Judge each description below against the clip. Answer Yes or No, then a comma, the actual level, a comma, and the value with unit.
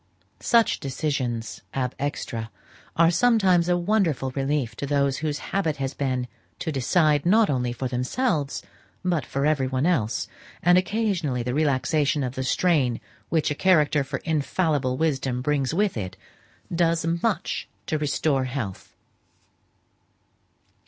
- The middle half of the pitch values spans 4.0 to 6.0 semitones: Yes, average, 4.4 semitones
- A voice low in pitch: No, medium, 145 Hz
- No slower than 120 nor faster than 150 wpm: Yes, average, 140 wpm